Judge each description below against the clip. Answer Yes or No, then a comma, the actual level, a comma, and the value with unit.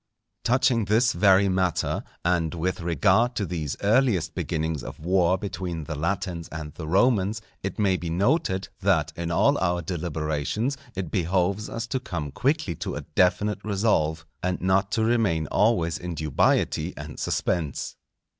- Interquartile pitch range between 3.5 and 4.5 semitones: Yes, average, 3.8 semitones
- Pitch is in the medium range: No, very low, 90 Hz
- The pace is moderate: Yes, average, 155 wpm